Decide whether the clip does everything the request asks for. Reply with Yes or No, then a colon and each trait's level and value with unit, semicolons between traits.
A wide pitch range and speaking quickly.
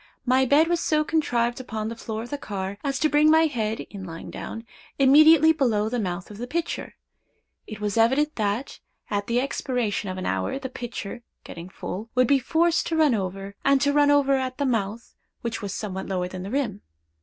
Yes: wide, 5.7 semitones; fast, 210 wpm